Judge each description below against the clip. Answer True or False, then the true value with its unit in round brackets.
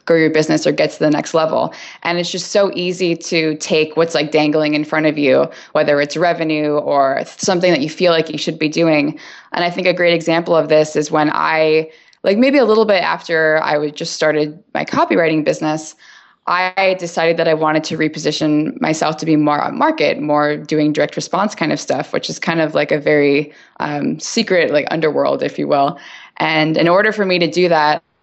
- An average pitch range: False (2.3 semitones)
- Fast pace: True (215 wpm)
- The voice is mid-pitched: True (160 Hz)